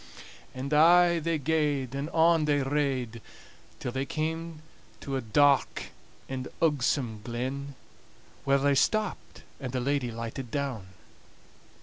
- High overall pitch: No, medium, 140 Hz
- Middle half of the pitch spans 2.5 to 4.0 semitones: Yes, average, 3.2 semitones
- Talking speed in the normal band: No, slow, 125 wpm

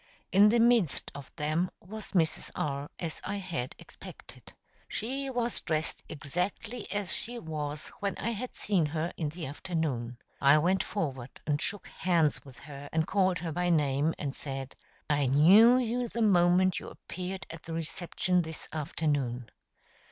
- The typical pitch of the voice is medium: Yes, medium, 165 Hz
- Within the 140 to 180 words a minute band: Yes, average, 160 wpm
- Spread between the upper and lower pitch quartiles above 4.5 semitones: Yes, average, 5.1 semitones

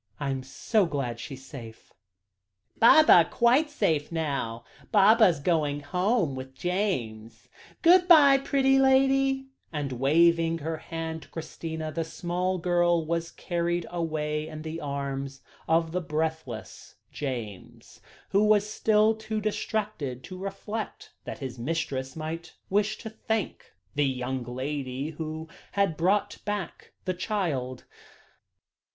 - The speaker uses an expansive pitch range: Yes, wide, 6.6 semitones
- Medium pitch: Yes, medium, 165 Hz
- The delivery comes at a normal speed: No, slow, 130 wpm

